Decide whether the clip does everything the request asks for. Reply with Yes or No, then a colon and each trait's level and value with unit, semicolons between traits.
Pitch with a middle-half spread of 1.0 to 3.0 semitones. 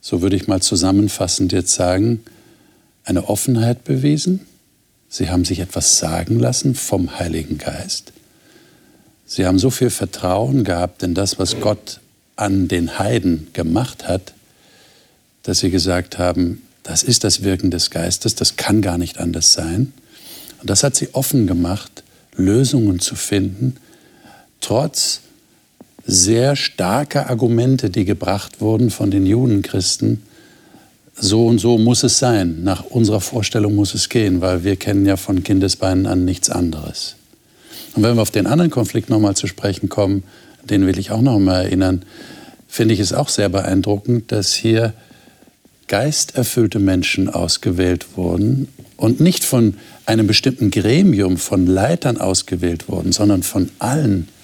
No: average, 4.1 semitones